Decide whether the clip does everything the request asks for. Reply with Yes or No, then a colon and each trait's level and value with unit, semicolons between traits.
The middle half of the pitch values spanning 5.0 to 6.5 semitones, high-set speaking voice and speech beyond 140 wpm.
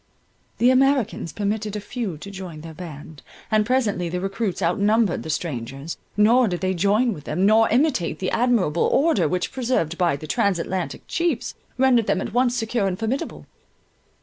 Yes: wide, 5.5 semitones; high, 200 Hz; average, 170 wpm